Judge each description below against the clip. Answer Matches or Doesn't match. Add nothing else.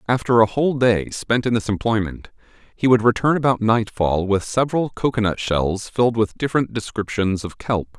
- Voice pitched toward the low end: Matches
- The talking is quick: Doesn't match